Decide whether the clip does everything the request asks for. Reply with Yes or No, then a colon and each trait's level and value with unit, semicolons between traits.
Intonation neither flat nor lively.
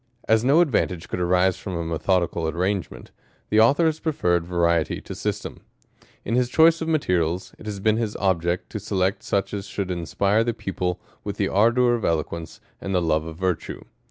Yes: average, 4.5 semitones